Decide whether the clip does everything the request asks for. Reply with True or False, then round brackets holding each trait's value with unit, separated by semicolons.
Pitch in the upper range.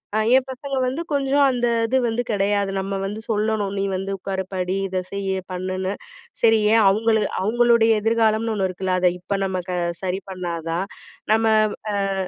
True (205 Hz)